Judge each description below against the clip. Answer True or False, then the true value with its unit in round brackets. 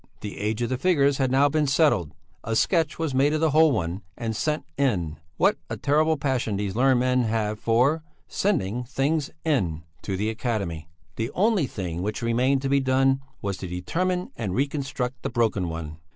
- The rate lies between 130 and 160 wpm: False (190 wpm)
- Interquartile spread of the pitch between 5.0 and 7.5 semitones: True (5.4 semitones)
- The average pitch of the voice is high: False (125 Hz)